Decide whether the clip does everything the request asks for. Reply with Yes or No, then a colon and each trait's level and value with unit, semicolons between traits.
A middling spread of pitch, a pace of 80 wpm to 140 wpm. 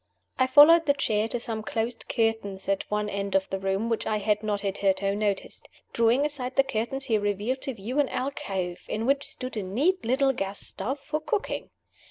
No: average, 5.0 semitones; average, 200 wpm